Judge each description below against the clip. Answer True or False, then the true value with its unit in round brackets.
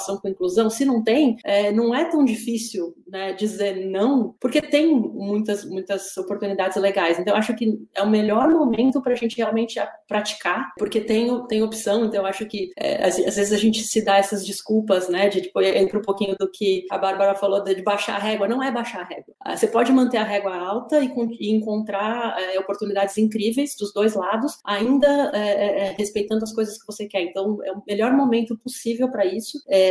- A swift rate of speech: True (205 wpm)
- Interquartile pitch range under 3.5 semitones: True (2.8 semitones)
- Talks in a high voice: True (210 Hz)